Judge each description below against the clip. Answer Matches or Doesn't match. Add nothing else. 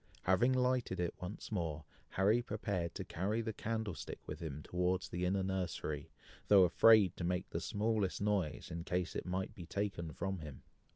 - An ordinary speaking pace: Matches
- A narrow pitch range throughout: Doesn't match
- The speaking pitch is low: Matches